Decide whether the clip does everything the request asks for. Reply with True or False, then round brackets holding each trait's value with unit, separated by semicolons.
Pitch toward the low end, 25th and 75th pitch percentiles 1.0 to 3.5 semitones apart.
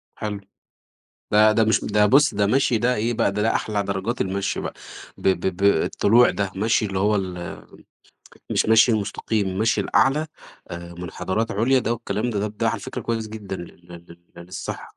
True (105 Hz; 2.7 semitones)